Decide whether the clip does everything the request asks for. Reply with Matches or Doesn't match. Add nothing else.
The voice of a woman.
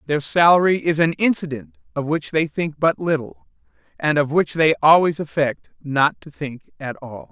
Doesn't match